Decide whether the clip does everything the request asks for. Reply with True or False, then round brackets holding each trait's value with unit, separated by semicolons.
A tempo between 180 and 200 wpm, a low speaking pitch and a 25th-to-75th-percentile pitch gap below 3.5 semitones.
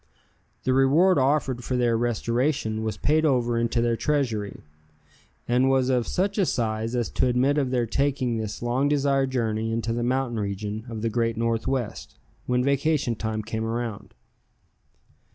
False (160 wpm; 120 Hz; 2.9 semitones)